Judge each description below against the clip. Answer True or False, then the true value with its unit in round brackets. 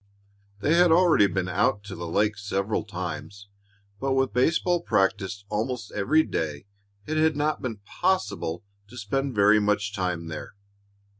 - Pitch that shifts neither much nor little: False (5.7 semitones)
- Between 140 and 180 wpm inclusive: True (150 wpm)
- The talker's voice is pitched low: True (105 Hz)